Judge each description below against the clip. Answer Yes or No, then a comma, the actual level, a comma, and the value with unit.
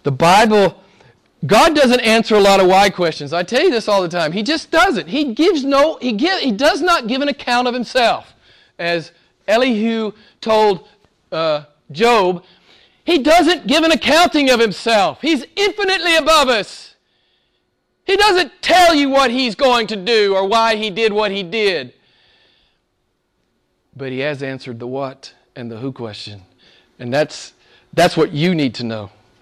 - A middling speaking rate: Yes, average, 170 wpm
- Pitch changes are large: Yes, wide, 8.9 semitones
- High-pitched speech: Yes, high, 220 Hz